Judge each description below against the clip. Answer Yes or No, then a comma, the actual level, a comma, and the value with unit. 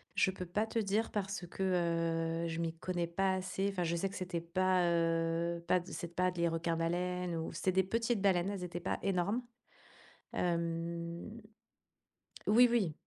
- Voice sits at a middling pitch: Yes, medium, 180 Hz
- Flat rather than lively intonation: Yes, narrow, 2.2 semitones